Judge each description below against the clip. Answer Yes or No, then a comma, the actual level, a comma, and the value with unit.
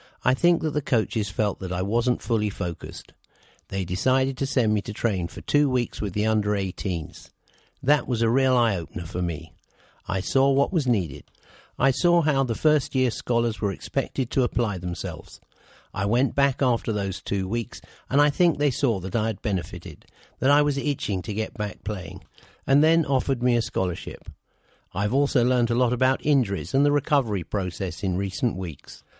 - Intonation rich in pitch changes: Yes, wide, 5.8 semitones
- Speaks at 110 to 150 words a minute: No, average, 195 wpm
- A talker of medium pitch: No, low, 115 Hz